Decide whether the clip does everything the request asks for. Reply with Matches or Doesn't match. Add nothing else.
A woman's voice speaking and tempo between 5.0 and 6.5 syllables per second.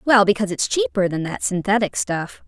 Matches